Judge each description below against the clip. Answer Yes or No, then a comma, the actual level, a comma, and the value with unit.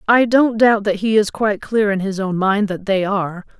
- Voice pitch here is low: No, high, 205 Hz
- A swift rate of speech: Yes, fast, 250 wpm